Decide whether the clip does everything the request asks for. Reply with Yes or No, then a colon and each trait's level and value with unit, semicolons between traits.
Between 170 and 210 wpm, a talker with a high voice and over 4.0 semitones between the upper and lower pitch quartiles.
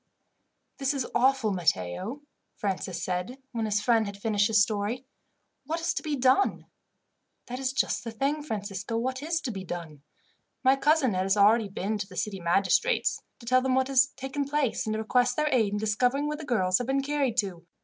Yes: average, 200 wpm; high, 235 Hz; average, 5.0 semitones